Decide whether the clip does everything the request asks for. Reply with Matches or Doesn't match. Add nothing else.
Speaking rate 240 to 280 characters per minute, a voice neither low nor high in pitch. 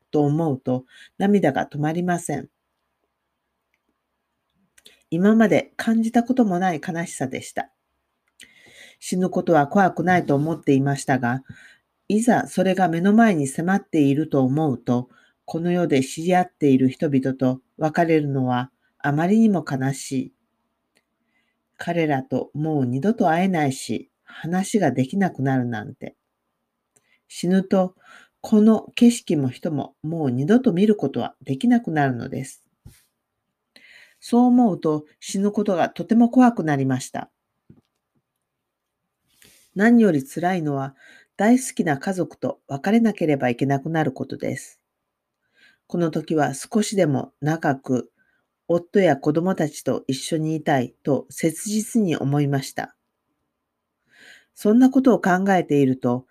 Matches